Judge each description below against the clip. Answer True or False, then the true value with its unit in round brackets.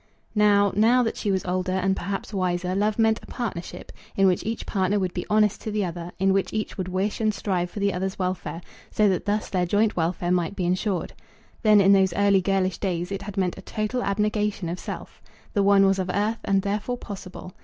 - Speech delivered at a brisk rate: True (220 wpm)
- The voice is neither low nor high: False (195 Hz)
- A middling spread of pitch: False (2.2 semitones)